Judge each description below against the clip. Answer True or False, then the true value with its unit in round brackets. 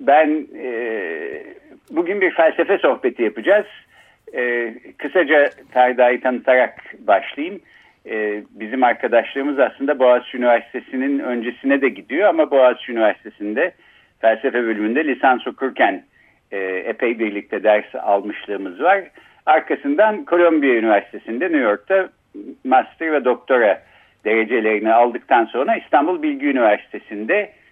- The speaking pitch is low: True (130 Hz)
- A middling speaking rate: True (105 wpm)